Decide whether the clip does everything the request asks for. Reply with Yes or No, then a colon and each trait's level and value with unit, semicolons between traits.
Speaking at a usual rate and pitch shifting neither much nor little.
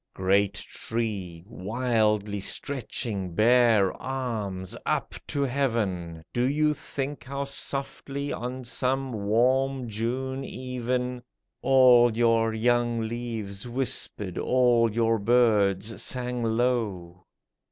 No: slow, 100 wpm; average, 3.4 semitones